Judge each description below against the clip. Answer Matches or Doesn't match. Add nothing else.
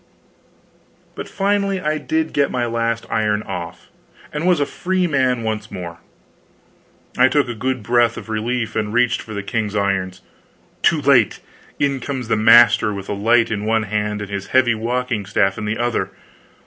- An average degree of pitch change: Matches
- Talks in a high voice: Doesn't match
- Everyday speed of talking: Matches